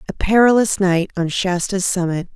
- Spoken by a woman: Yes, female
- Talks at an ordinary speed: Yes, average, 155 wpm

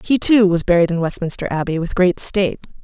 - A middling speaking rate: No, fast, 210 wpm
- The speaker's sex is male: No, female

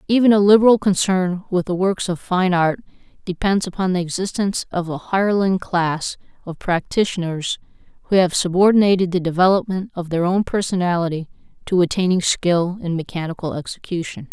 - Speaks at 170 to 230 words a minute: No, average, 145 wpm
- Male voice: No, female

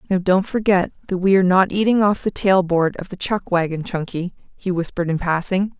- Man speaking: No, female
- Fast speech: Yes, fast, 215 wpm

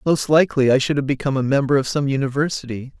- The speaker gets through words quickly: Yes, fast, 220 wpm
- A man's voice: Yes, male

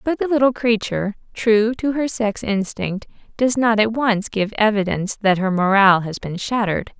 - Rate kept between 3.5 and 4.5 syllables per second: No, 5.0 syllables/s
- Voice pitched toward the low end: No, high, 215 Hz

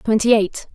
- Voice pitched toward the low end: No, high, 220 Hz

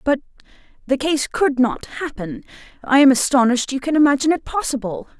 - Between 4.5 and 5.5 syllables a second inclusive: No, 5.9 syllables/s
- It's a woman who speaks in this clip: Yes, female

